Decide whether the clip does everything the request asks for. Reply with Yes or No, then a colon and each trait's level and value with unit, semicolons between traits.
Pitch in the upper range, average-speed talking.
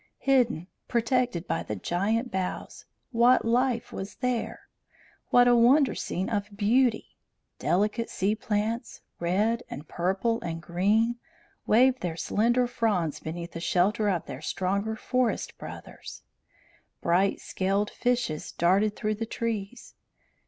No: high, 215 Hz; slow, 125 wpm